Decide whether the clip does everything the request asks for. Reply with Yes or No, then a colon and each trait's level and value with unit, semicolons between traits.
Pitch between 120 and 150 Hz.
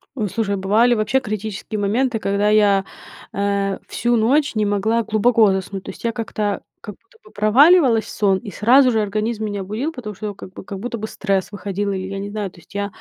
No: high, 210 Hz